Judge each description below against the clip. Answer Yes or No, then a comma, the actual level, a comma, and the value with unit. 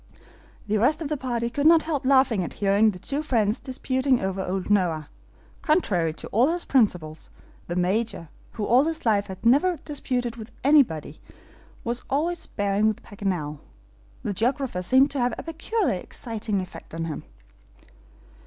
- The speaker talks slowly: No, average, 160 wpm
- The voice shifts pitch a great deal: Yes, wide, 6.3 semitones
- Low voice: No, high, 230 Hz